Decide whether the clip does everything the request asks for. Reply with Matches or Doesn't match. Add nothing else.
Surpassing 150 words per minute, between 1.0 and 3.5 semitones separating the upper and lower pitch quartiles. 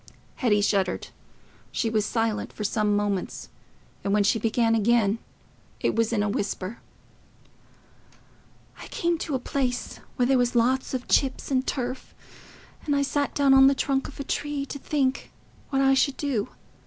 Doesn't match